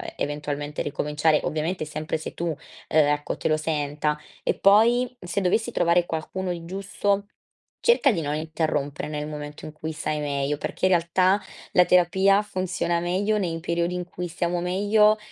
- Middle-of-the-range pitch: Yes, medium, 170 Hz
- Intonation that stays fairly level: No, average, 3.8 semitones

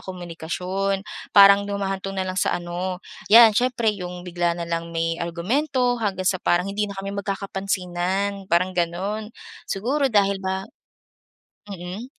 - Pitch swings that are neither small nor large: No, narrow, 2.2 semitones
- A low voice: No, high, 195 Hz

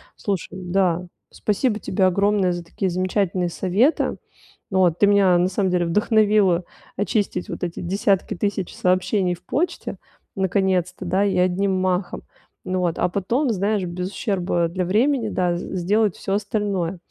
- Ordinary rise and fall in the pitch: No, narrow, 2.2 semitones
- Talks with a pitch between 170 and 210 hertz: Yes, high, 190 Hz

